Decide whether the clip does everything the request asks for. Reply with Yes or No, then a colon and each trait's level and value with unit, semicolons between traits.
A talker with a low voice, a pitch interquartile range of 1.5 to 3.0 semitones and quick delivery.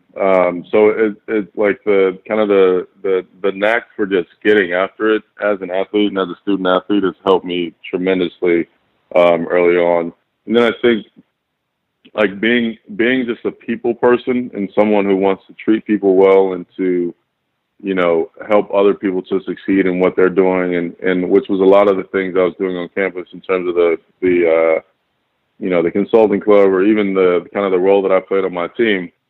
Yes: very low, 95 Hz; narrow, 2.5 semitones; fast, 210 wpm